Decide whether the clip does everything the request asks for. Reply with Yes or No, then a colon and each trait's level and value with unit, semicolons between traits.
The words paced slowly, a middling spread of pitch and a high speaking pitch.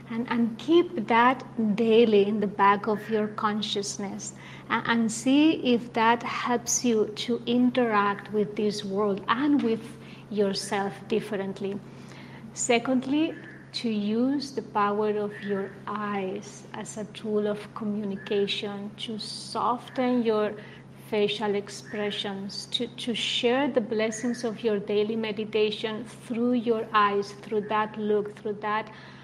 No: slow, 125 wpm; narrow, 2.1 semitones; high, 215 Hz